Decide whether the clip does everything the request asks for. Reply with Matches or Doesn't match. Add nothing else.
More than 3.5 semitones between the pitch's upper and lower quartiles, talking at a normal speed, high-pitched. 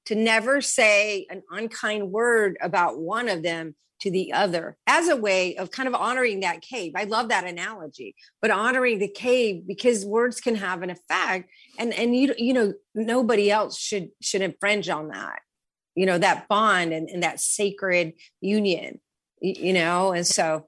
Matches